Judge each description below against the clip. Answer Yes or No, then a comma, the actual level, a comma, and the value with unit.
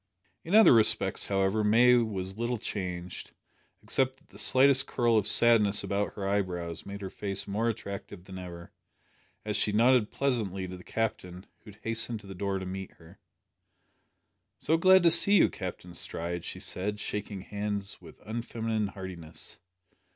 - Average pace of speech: Yes, average, 165 wpm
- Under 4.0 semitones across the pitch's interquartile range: Yes, average, 3.5 semitones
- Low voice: Yes, low, 105 Hz